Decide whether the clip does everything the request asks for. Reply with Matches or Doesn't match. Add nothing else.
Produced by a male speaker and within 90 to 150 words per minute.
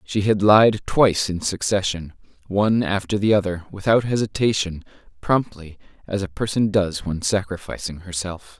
Matches